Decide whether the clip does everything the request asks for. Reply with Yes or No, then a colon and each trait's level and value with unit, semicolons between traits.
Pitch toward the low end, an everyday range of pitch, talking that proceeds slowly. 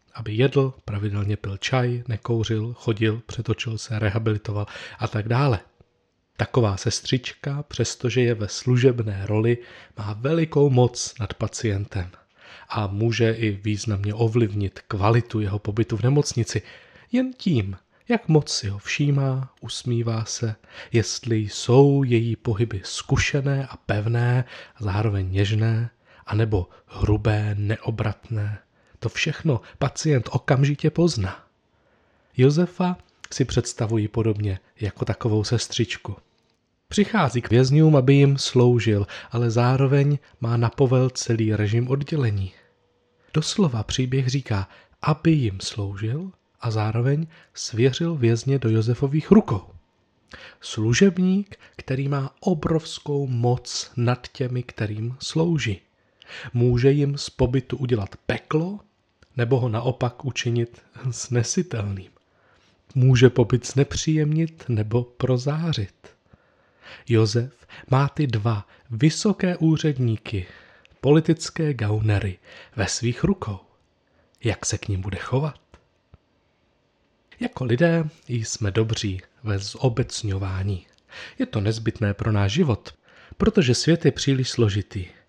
Yes: low, 120 Hz; average, 4.4 semitones; slow, 110 wpm